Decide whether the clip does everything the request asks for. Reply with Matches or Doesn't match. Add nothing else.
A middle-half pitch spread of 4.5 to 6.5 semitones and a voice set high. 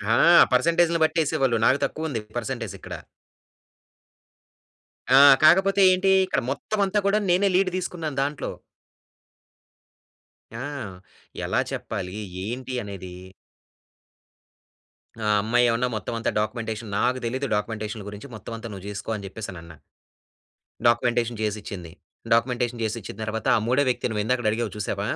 Doesn't match